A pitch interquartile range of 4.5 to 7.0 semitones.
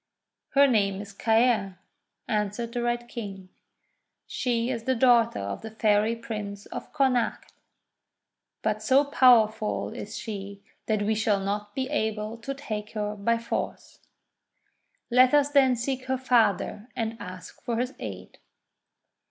No: average, 3.0 semitones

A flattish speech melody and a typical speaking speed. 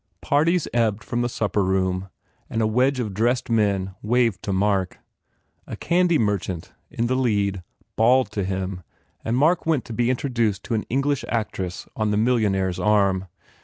No: average, 4.2 semitones; average, 170 wpm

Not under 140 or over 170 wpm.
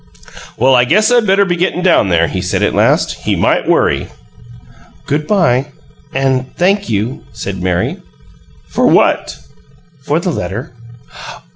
Yes: average, 145 wpm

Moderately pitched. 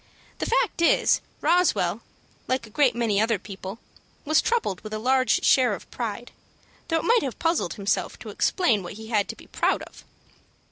No: high, 235 Hz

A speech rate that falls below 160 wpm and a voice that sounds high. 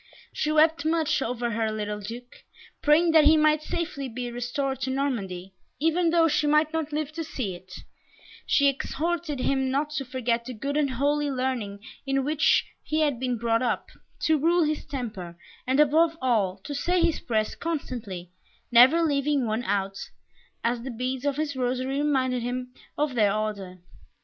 No: average, 175 wpm; very high, 270 Hz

